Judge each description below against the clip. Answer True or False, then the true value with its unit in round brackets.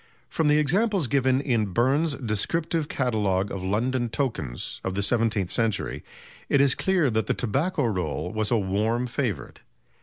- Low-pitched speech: True (120 Hz)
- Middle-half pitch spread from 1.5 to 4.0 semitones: False (5.4 semitones)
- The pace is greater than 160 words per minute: False (155 wpm)